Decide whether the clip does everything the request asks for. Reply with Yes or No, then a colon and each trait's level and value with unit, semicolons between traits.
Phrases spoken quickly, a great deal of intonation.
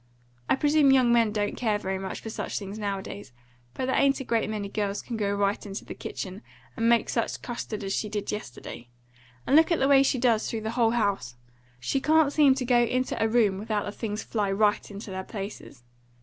No: fast, 225 wpm; average, 3.7 semitones